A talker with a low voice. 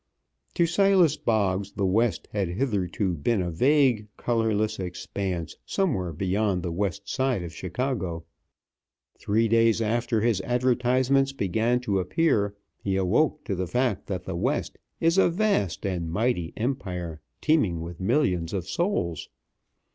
Yes: low, 105 Hz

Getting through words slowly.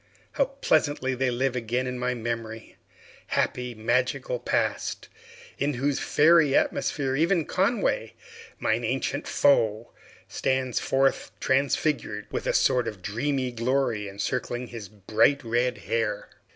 Yes: slow, 125 wpm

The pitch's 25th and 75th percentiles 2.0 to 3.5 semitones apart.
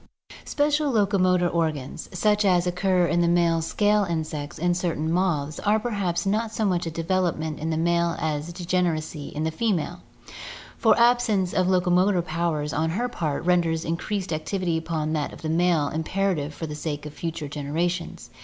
Yes: average, 3.0 semitones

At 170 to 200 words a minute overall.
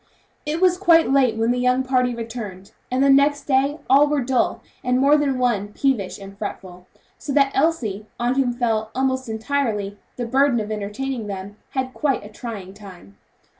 Yes: average, 180 wpm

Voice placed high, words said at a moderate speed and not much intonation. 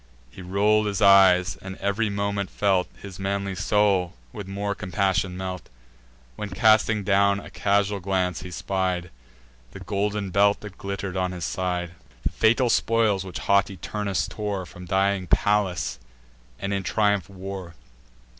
No: low, 100 Hz; average, 145 wpm; narrow, 1.7 semitones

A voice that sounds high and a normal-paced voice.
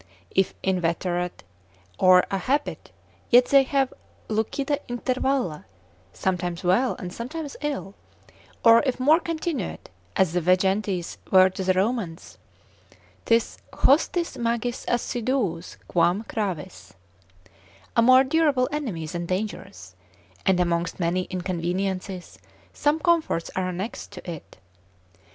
No: high, 195 Hz; slow, 115 wpm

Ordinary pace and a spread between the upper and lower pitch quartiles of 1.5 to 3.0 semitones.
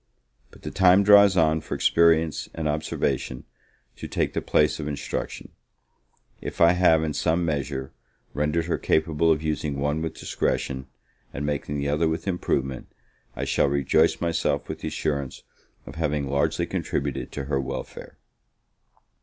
Yes: average, 155 wpm; narrow, 2.4 semitones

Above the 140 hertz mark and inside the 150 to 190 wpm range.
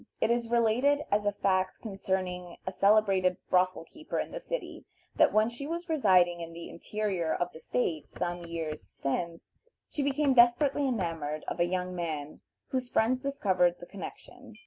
Yes: high, 190 Hz; average, 170 wpm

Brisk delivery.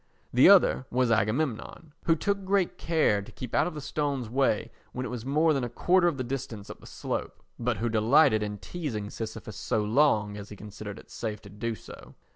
Yes: fast, 215 wpm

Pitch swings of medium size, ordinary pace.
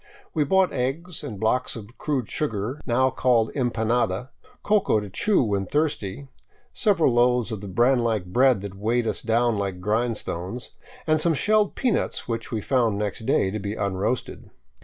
Yes: average, 4.4 semitones; average, 165 wpm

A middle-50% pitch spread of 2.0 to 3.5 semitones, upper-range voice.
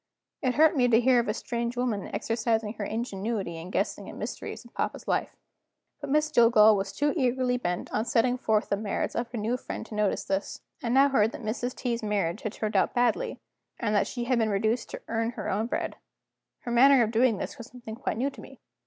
Yes: average, 2.7 semitones; high, 230 Hz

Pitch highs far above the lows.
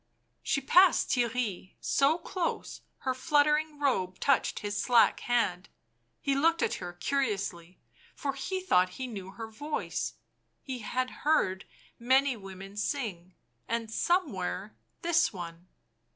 Yes: wide, 6.9 semitones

